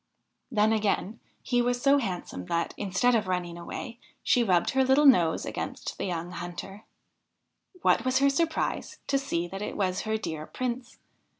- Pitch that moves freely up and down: Yes, wide, 6.1 semitones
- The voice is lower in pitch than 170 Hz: No, high, 215 Hz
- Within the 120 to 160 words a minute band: No, average, 170 wpm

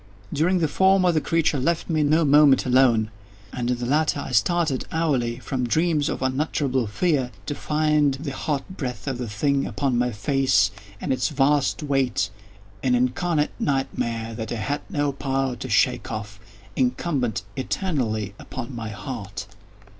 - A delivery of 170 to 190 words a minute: No, average, 155 wpm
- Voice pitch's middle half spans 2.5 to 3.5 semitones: No, average, 4.1 semitones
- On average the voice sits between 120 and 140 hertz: Yes, low, 135 Hz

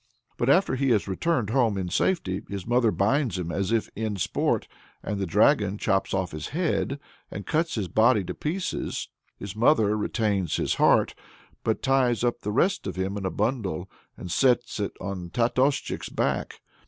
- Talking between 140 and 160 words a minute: No, average, 180 wpm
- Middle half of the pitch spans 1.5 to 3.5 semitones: No, average, 5.1 semitones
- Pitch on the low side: Yes, low, 110 Hz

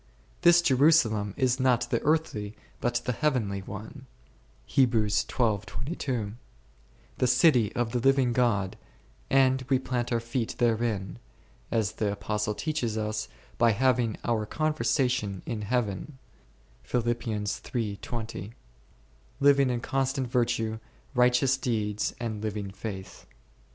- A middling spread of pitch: Yes, average, 3.5 semitones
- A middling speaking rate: No, slow, 110 wpm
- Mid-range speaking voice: No, low, 120 Hz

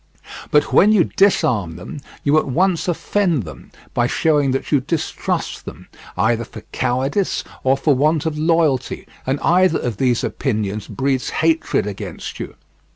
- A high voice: No, medium, 140 Hz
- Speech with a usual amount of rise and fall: Yes, average, 4.8 semitones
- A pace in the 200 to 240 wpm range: No, average, 155 wpm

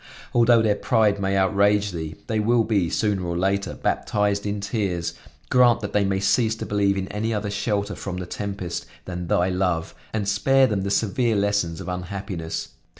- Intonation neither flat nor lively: No, narrow, 2.1 semitones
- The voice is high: No, low, 100 Hz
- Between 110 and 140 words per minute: No, average, 185 wpm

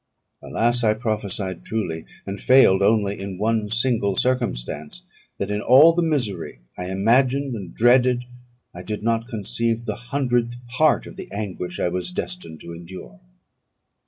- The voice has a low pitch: Yes, low, 110 Hz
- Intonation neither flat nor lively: Yes, average, 4.3 semitones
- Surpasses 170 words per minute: No, average, 150 wpm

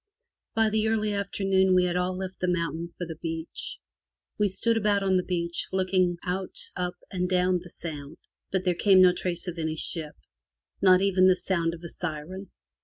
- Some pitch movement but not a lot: No, narrow, 1.9 semitones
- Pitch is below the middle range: No, medium, 180 Hz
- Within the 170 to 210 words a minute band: Yes, average, 190 wpm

